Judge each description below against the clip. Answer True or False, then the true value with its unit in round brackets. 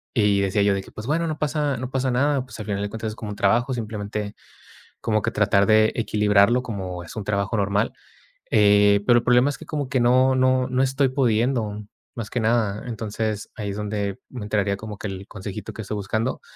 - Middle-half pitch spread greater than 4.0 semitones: False (3.6 semitones)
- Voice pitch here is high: False (110 Hz)